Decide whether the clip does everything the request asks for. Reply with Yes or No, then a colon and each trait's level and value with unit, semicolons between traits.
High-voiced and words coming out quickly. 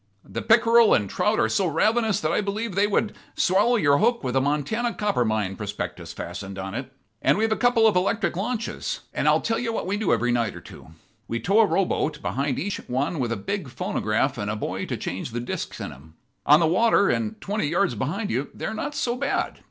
No: medium, 180 Hz; fast, 230 wpm